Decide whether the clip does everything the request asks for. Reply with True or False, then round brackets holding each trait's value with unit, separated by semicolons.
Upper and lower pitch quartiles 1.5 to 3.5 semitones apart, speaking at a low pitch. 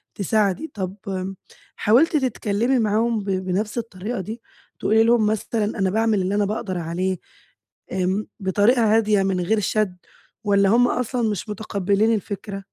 False (2.7 semitones; 210 Hz)